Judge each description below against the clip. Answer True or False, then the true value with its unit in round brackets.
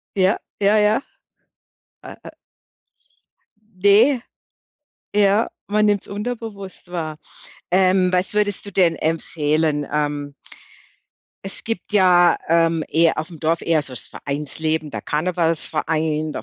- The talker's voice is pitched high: False (175 Hz)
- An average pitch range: True (4.3 semitones)